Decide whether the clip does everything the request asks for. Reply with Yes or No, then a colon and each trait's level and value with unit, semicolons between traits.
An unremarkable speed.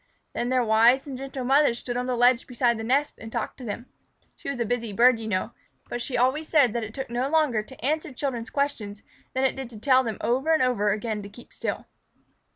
No: fast, 240 wpm